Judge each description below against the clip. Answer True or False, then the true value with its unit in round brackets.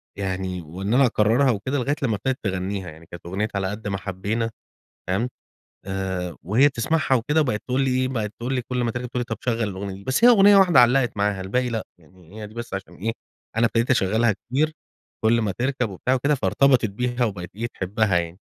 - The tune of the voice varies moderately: True (4.6 semitones)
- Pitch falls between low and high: False (110 Hz)